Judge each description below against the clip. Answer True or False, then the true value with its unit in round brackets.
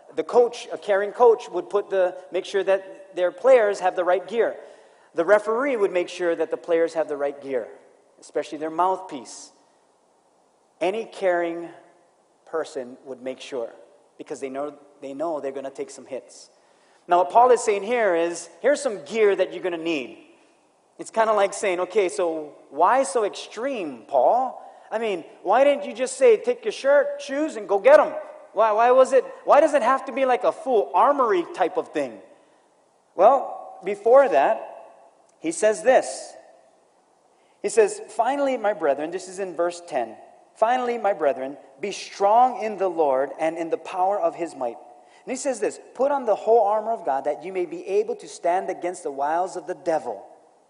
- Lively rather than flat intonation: True (8.0 semitones)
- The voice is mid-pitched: False (200 Hz)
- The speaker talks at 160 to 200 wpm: True (190 wpm)